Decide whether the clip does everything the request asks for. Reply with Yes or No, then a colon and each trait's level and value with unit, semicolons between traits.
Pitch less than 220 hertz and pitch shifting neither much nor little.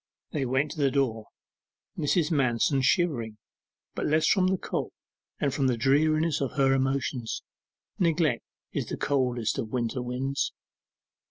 Yes: low, 135 Hz; average, 3.5 semitones